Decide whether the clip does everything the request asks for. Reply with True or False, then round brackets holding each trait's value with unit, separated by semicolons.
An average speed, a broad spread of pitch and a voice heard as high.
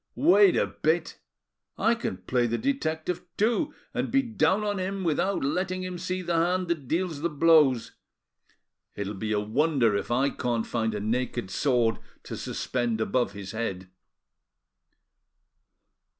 False (150 wpm; 7.9 semitones; 150 Hz)